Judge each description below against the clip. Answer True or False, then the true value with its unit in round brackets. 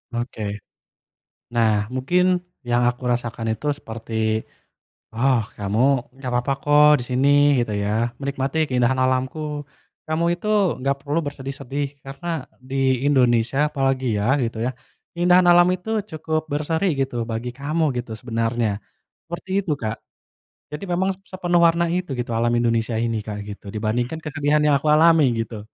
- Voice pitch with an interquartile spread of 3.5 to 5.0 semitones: True (4.7 semitones)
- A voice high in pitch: False (135 Hz)